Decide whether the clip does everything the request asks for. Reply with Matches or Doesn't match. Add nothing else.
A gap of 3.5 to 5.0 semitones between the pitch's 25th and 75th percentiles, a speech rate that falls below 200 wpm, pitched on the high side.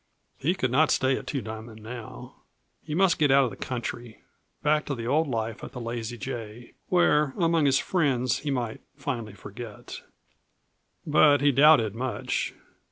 Doesn't match